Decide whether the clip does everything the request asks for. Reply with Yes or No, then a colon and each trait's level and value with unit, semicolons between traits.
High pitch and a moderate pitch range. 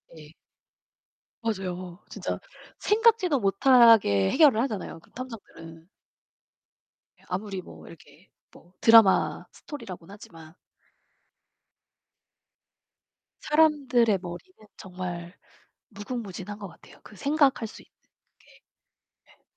No: high, 205 Hz; wide, 6.1 semitones